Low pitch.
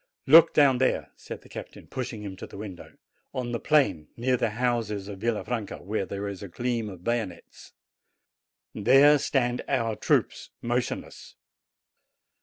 Yes: low, 115 Hz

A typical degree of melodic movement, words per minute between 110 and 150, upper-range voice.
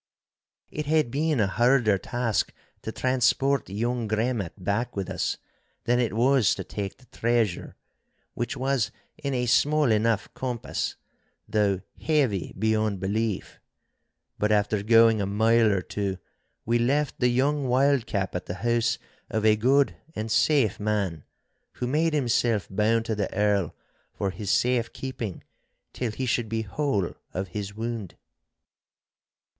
No: average, 3.5 semitones; average, 140 wpm; low, 115 Hz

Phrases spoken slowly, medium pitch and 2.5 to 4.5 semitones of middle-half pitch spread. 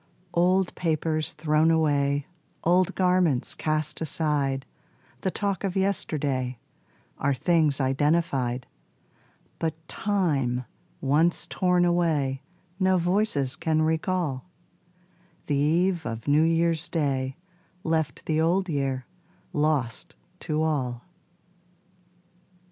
Yes: slow, 100 wpm; medium, 155 Hz; average, 3.8 semitones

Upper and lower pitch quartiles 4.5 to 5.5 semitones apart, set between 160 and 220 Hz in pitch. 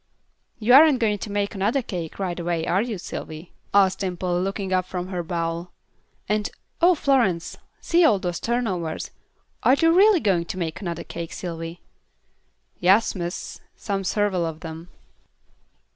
No: average, 3.8 semitones; medium, 185 Hz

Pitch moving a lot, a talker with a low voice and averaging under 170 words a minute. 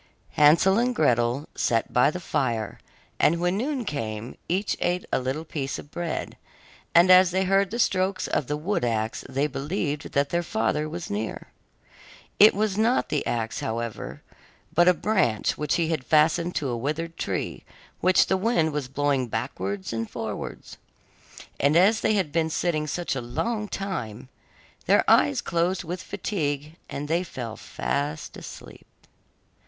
No: wide, 5.8 semitones; medium, 155 Hz; average, 160 wpm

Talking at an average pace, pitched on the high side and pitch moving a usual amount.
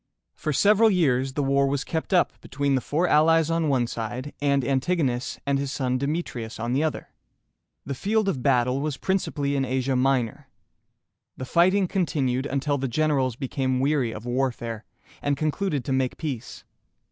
No: average, 175 wpm; medium, 140 Hz; average, 3.2 semitones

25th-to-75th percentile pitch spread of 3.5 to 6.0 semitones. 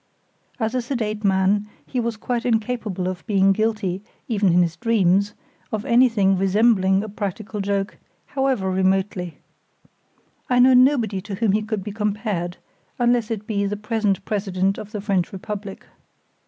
No: average, 2.7 semitones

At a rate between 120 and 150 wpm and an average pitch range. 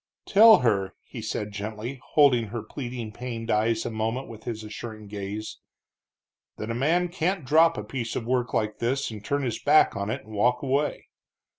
No: average, 185 wpm; average, 4.0 semitones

